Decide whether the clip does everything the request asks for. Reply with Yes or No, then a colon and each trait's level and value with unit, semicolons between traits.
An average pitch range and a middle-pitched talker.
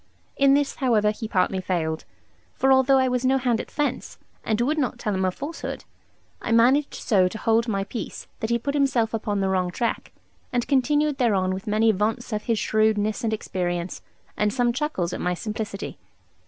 No: average, 4.5 semitones; high, 225 Hz